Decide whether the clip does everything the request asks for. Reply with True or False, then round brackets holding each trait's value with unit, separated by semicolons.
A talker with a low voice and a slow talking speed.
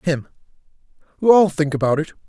False (165 Hz; 130 wpm)